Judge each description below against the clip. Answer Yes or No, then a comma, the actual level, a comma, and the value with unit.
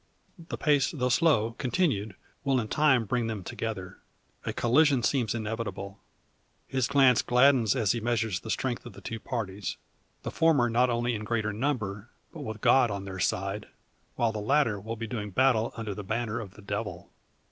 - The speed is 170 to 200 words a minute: Yes, average, 180 wpm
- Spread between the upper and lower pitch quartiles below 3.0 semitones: No, average, 3.3 semitones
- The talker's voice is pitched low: Yes, low, 115 Hz